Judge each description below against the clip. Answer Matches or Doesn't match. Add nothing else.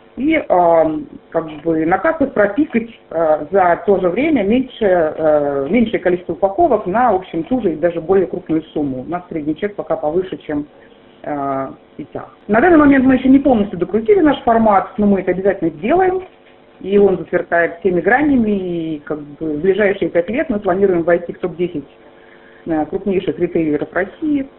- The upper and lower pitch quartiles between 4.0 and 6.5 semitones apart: Matches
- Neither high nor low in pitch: Matches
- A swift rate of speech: Matches